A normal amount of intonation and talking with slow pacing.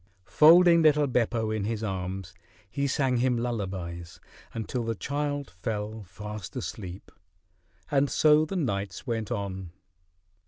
No: wide, 6.2 semitones; slow, 125 wpm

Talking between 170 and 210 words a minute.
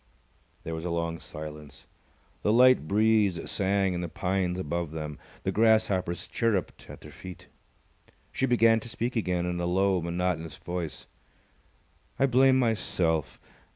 No: average, 145 wpm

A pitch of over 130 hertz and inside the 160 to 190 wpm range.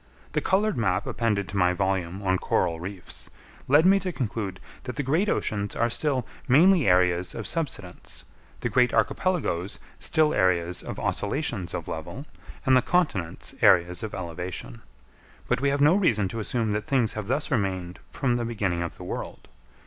No: low, 110 Hz; average, 170 wpm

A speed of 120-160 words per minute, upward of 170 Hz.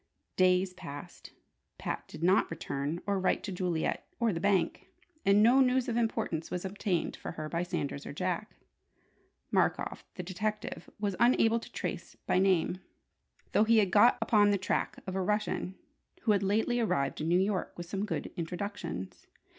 No: average, 170 wpm; high, 190 Hz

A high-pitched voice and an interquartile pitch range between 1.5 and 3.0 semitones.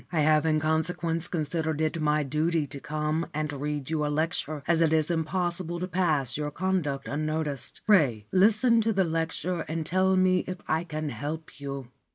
No: medium, 160 Hz; narrow, 2.5 semitones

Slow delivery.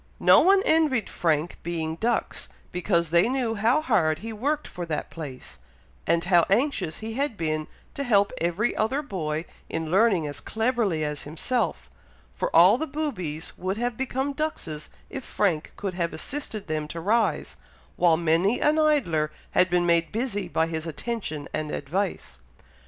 No: average, 165 wpm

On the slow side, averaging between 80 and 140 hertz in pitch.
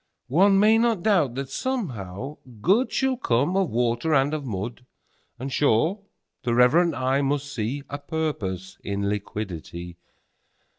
Yes: slow, 120 wpm; low, 135 Hz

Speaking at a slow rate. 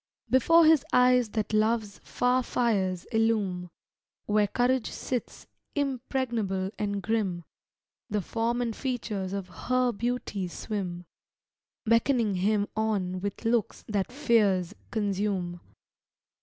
Yes: slow, 110 wpm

